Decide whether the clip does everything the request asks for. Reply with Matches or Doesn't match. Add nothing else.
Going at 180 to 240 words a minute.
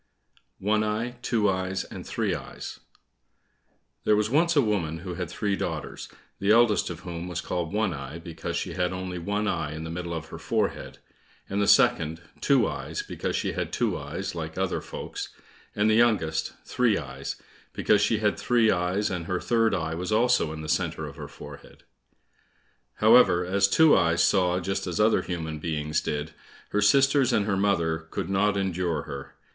Matches